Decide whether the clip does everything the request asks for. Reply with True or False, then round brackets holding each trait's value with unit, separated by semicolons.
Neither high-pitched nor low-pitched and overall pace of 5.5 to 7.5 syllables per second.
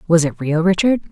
True (175 Hz; 5.7 syllables/s)